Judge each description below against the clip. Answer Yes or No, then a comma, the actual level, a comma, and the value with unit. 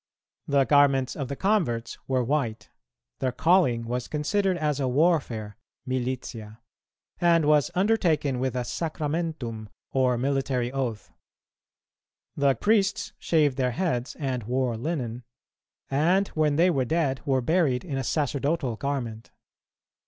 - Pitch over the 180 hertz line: No, low, 135 Hz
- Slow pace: Yes, slow, 130 wpm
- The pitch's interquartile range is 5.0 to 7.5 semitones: No, average, 4.2 semitones